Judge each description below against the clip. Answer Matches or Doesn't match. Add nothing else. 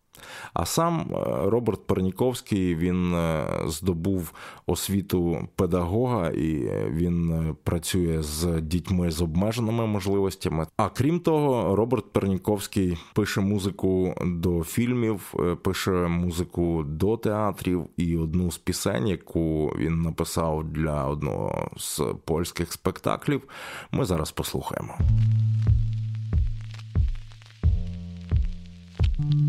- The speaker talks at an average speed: Doesn't match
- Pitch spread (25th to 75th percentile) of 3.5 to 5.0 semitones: Matches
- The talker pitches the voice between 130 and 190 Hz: Doesn't match